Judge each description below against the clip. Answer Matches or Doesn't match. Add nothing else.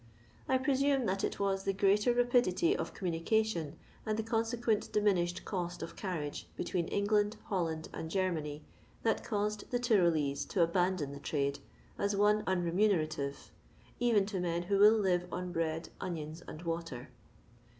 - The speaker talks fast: Doesn't match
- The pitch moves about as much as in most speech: Matches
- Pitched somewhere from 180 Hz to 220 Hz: Matches